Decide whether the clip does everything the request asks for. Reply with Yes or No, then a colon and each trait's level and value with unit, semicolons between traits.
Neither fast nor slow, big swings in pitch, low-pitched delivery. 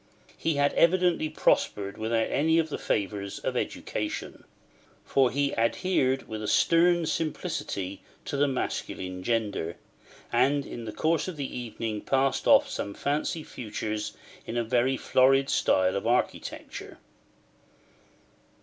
No: slow, 130 wpm; wide, 5.7 semitones; low, 130 Hz